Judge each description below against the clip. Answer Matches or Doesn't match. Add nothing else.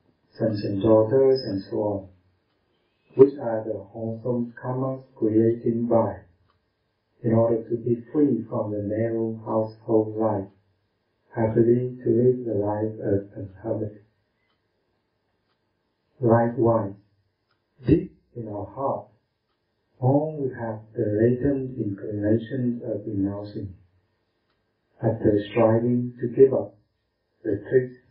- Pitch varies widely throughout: Doesn't match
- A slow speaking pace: Matches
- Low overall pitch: Matches